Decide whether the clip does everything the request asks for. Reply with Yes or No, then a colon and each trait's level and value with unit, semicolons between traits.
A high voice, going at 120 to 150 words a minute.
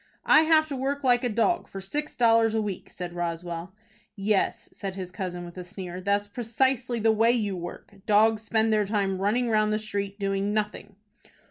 No: high, 210 Hz; average, 195 wpm